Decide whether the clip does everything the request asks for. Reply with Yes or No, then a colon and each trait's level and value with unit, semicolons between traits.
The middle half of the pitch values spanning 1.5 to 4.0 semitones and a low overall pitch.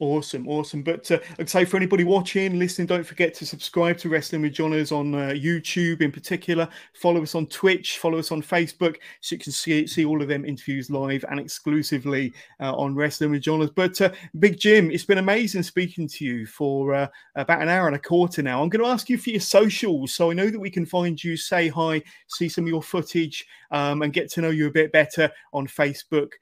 No: average, 3.2 semitones; medium, 165 Hz